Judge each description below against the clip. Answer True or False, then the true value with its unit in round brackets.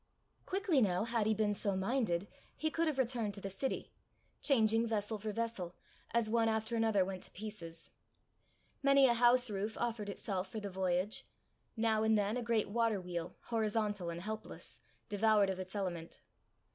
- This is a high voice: True (215 Hz)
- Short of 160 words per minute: False (170 wpm)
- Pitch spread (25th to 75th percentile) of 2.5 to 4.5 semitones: True (3.0 semitones)